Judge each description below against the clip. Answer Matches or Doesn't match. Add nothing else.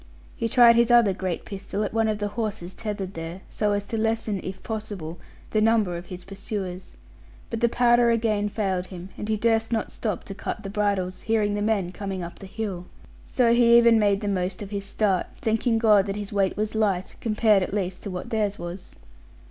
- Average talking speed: Doesn't match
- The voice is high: Matches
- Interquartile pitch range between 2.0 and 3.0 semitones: Matches